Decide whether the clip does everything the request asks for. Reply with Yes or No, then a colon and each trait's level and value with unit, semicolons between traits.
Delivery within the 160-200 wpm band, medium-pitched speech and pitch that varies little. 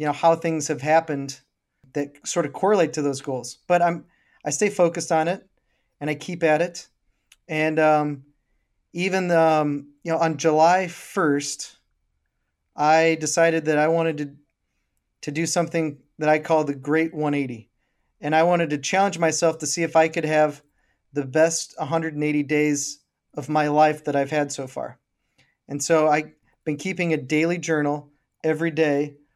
Yes: average, 170 wpm; medium, 155 Hz; narrow, 2.1 semitones